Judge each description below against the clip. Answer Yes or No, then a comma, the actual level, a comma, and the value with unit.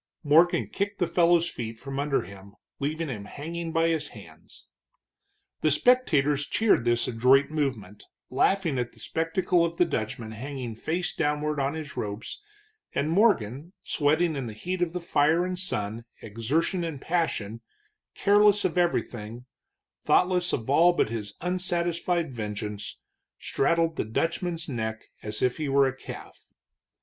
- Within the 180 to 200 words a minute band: No, average, 150 wpm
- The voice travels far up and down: Yes, wide, 6.6 semitones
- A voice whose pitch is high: No, medium, 150 Hz